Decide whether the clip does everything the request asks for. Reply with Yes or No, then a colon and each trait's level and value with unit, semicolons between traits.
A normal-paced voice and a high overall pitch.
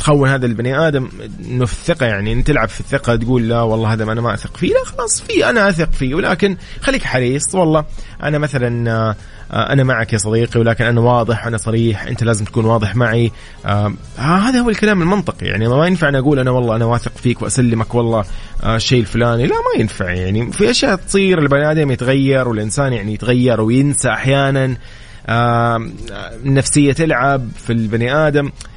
No: average, 185 wpm; low, 120 Hz